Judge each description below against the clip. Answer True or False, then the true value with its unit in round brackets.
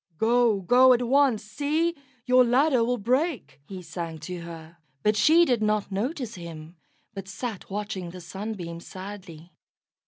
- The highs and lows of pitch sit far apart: True (5.8 semitones)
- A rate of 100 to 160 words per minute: True (150 wpm)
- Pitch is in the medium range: False (210 Hz)